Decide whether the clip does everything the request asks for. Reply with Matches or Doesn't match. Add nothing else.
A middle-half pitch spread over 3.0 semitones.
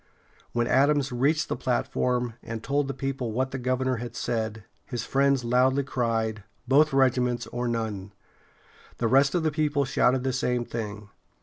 Doesn't match